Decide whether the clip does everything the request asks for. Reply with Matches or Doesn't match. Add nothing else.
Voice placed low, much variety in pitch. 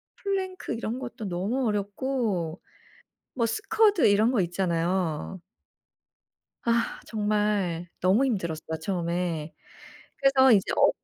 Doesn't match